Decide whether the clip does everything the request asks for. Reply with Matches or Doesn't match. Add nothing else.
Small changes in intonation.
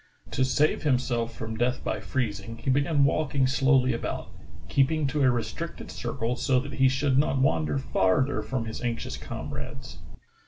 Doesn't match